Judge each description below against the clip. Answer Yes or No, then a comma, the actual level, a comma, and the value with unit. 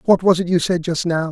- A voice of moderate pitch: Yes, medium, 175 Hz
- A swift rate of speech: Yes, fast, 320 wpm